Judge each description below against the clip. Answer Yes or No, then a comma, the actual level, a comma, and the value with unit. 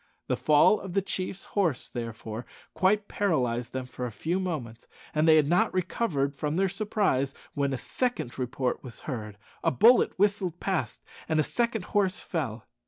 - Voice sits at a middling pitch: Yes, medium, 155 Hz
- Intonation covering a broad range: Yes, wide, 7.2 semitones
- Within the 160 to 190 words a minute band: Yes, average, 170 wpm